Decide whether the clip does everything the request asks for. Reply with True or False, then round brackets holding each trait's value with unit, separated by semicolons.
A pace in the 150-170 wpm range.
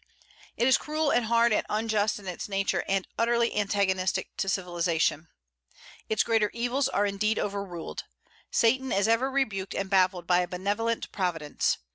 True (155 wpm)